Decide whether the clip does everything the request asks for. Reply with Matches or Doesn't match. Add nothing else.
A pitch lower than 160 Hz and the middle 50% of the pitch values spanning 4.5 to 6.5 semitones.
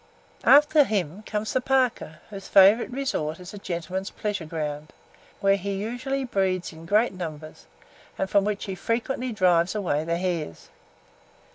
Doesn't match